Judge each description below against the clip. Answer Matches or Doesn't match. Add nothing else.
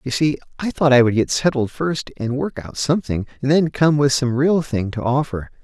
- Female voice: Doesn't match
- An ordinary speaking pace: Doesn't match